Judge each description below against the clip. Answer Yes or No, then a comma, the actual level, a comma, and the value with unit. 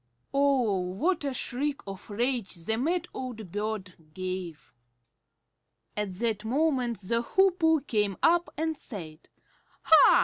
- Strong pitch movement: Yes, wide, 6.6 semitones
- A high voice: Yes, high, 235 Hz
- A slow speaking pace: Yes, slow, 125 wpm